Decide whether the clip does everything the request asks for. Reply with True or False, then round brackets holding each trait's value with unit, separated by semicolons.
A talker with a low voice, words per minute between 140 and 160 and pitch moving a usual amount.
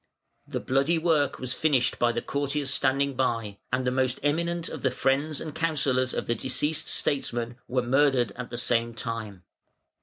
False (130 Hz; 175 wpm; 3.2 semitones)